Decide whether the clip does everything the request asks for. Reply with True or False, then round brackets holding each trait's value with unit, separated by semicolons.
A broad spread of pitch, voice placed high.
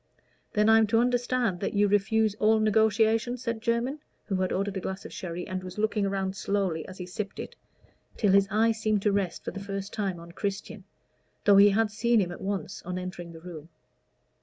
False (2.7 semitones; 200 Hz)